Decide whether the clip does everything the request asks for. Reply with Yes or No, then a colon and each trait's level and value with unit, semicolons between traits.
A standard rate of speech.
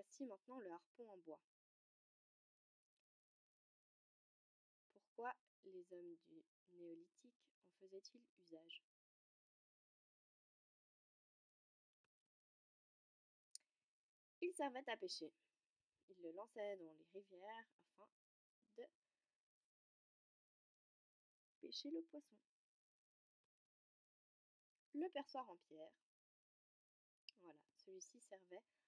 No: slow, 75 wpm